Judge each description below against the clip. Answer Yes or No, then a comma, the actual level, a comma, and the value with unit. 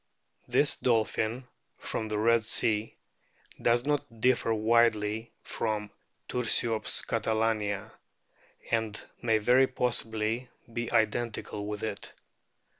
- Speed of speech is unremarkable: No, slow, 100 wpm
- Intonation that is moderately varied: No, narrow, 1.7 semitones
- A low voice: Yes, low, 110 Hz